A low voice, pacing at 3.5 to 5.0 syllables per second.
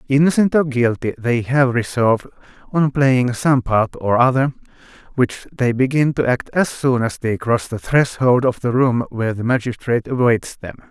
Yes: low, 125 Hz; 4.8 syllables/s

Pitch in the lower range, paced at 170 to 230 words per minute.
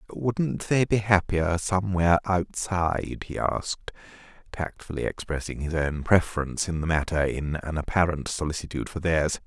No: very low, 85 Hz; average, 140 wpm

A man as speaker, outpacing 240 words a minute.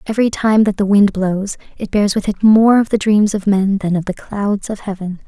No: female; fast, 250 wpm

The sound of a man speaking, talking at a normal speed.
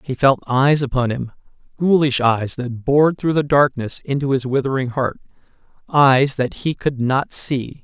Yes: male; average, 155 wpm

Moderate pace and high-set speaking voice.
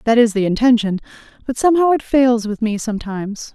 Yes: average, 185 wpm; high, 230 Hz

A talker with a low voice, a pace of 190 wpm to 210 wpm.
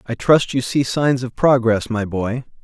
Yes: low, 125 Hz; fast, 205 wpm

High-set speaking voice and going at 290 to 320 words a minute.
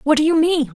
Yes: very high, 295 Hz; fast, 305 wpm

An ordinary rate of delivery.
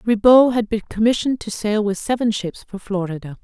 Yes: average, 190 wpm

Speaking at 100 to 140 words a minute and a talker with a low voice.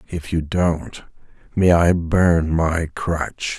Yes: slow, 135 wpm; very low, 85 Hz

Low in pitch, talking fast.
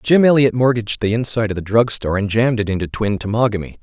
Yes: low, 110 Hz; fast, 235 wpm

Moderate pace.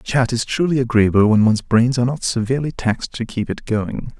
No: fast, 215 wpm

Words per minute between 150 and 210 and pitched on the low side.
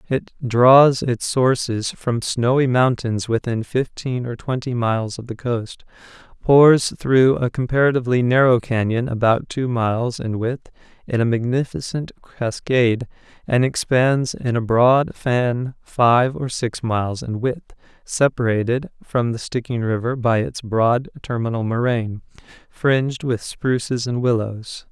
No: slow, 135 wpm; low, 120 Hz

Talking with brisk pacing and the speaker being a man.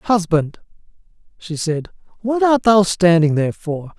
No: slow, 135 wpm; male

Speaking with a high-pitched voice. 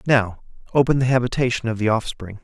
No: low, 120 Hz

